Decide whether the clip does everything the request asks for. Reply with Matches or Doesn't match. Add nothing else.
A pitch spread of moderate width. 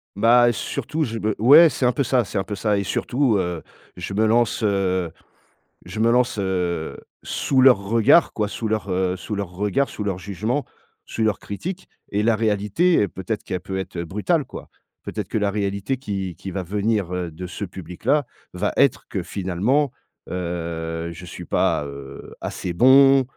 Matches